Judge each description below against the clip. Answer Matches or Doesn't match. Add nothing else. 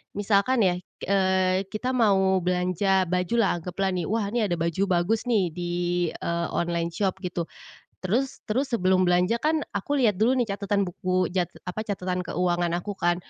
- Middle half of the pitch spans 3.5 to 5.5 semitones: Doesn't match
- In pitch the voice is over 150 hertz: Matches